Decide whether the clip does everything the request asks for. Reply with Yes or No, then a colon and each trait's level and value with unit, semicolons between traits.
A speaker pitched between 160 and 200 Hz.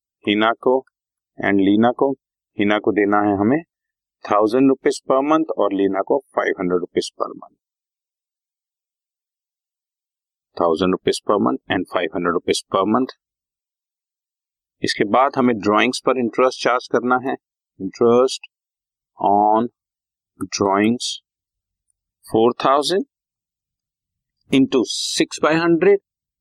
No: low, 110 Hz